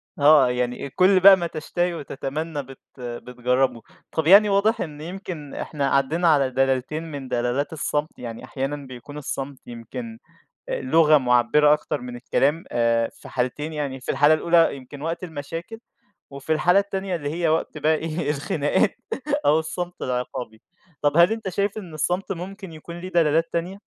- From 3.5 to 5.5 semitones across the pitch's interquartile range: Yes, average, 4.4 semitones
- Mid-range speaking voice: Yes, medium, 150 Hz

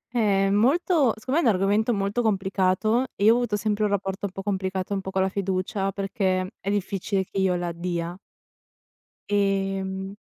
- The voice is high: Yes, high, 195 Hz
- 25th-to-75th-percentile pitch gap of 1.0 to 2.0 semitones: Yes, narrow, 1.7 semitones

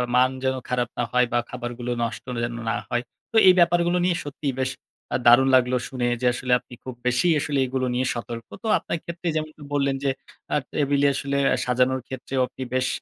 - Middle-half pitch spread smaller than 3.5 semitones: Yes, narrow, 2.5 semitones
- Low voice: Yes, low, 130 Hz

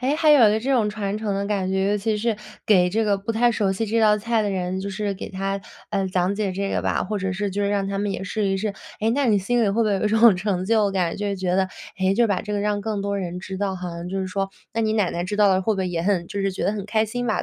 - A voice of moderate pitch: No, high, 200 Hz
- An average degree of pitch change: No, narrow, 2.1 semitones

